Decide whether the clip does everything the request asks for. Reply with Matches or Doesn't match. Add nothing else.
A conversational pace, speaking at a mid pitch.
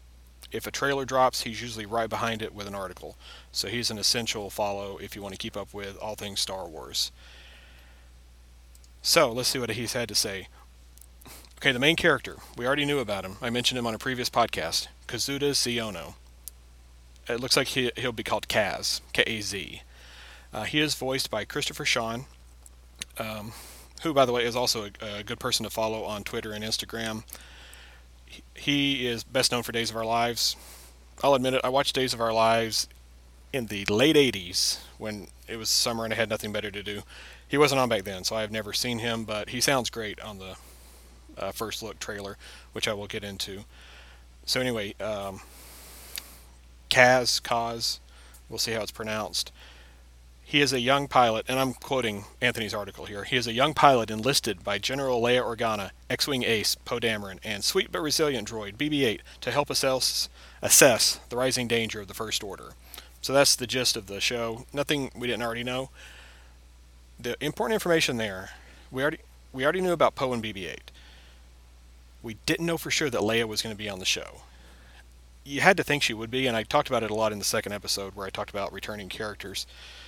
Doesn't match